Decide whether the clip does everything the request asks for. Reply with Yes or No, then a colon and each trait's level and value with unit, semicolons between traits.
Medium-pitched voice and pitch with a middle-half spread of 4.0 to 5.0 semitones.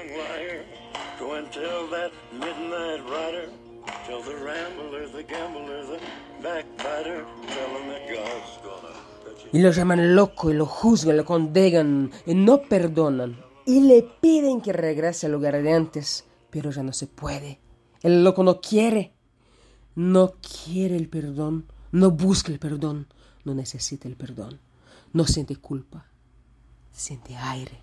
Yes: medium, 150 Hz; average, 4.7 semitones